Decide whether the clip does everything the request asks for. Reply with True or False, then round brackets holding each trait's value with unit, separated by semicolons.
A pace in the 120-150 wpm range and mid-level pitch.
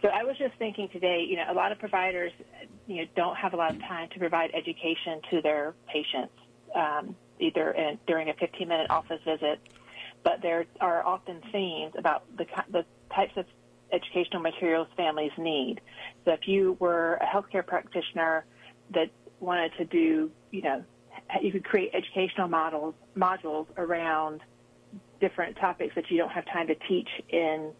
False (170 wpm; 170 Hz)